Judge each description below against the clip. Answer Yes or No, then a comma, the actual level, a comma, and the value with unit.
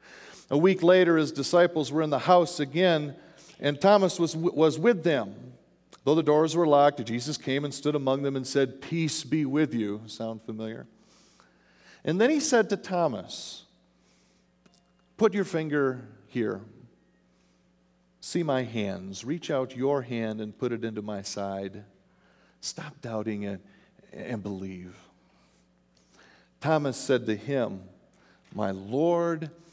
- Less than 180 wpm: Yes, average, 140 wpm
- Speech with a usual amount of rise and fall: No, wide, 7.7 semitones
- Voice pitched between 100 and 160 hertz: Yes, low, 135 Hz